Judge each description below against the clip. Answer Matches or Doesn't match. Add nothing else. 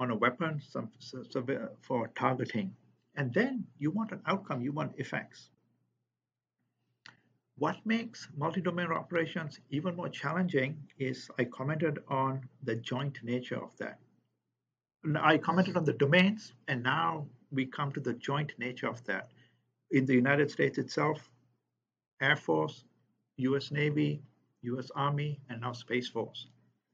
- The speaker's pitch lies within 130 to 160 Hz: Matches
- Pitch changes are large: Doesn't match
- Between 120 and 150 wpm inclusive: Matches